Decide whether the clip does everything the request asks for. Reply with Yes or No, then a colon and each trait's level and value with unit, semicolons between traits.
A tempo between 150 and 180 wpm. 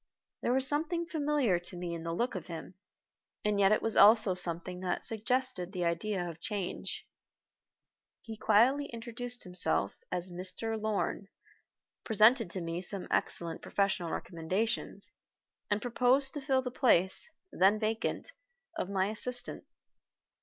No: average, 140 wpm